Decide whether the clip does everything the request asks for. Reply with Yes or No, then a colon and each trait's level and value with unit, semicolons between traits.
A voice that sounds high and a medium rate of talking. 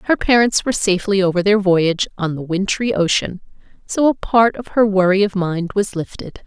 Yes: high, 200 Hz; average, 195 wpm